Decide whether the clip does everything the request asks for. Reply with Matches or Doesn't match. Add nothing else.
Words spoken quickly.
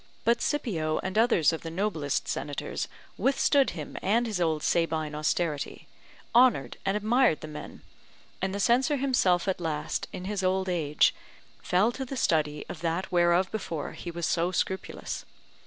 Doesn't match